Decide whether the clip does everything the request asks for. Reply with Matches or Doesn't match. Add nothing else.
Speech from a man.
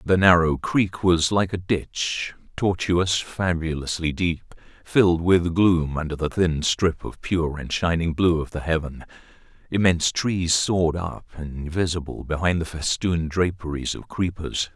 Matches